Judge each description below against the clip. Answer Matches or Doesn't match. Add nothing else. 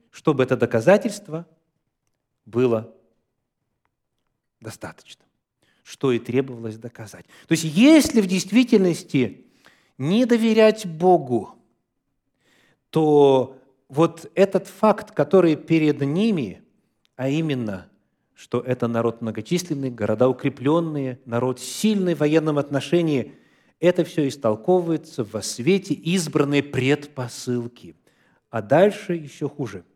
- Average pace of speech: Doesn't match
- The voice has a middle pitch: Matches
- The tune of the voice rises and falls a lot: Matches